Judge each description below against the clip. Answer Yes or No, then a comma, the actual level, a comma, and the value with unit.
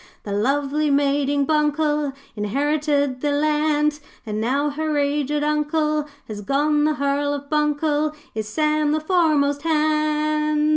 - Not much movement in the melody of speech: Yes, narrow, 1.3 semitones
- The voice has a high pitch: Yes, very high, 295 Hz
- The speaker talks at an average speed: No, slow, 130 wpm